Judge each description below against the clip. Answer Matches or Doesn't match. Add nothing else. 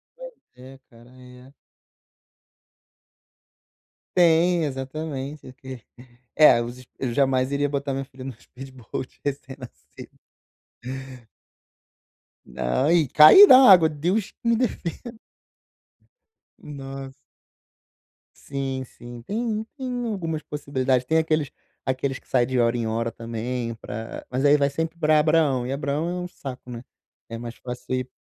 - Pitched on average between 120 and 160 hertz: Matches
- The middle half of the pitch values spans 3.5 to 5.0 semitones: Matches